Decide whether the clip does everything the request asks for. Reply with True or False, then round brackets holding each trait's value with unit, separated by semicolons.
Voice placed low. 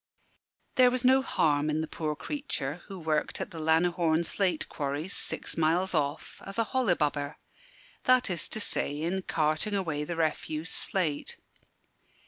False (165 Hz)